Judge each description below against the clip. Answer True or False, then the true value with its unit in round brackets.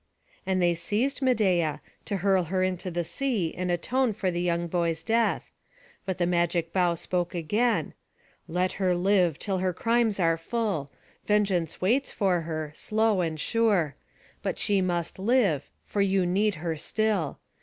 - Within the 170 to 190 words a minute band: False (160 wpm)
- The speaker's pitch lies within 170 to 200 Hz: True (185 Hz)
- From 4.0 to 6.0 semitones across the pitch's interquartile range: False (3.5 semitones)